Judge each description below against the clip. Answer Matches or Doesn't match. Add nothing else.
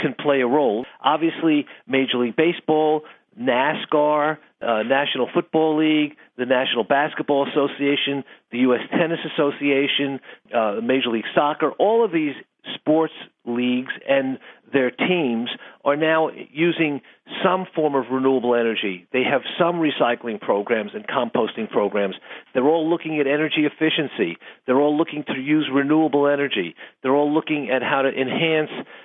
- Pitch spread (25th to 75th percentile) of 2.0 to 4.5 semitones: Matches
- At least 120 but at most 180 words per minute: Matches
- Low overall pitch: Doesn't match